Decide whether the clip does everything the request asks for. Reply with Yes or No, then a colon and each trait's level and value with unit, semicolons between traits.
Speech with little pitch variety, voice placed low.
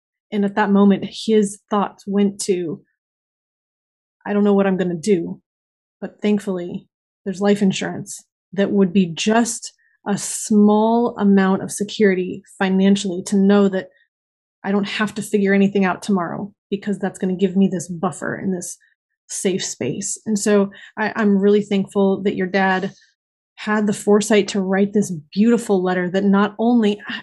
No: narrow, 1.4 semitones; high, 200 Hz